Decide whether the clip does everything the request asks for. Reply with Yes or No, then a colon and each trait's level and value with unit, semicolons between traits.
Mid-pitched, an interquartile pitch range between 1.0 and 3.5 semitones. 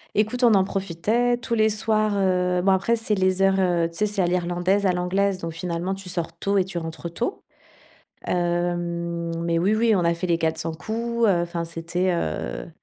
Yes: medium, 180 Hz; average, 2.9 semitones